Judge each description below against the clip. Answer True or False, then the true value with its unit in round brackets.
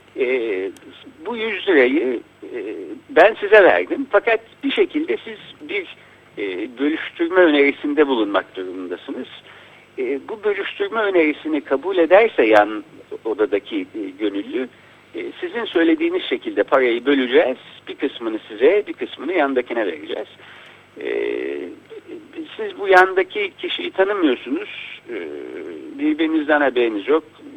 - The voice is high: True (345 Hz)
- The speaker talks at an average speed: True (110 wpm)